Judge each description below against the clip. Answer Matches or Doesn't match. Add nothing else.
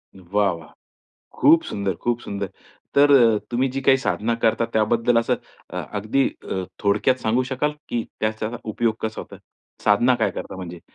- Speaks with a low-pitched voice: Matches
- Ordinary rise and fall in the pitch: Matches